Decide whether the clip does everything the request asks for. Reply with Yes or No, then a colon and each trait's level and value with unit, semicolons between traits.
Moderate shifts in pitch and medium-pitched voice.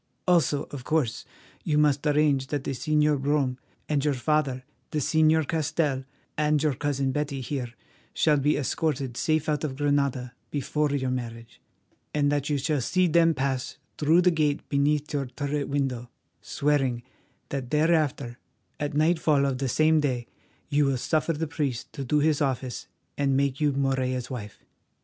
No: narrow, 2.3 semitones; medium, 145 Hz